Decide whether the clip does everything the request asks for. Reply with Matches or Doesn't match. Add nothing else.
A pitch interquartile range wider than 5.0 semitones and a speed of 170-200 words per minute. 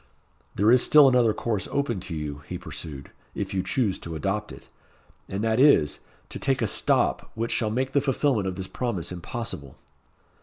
Matches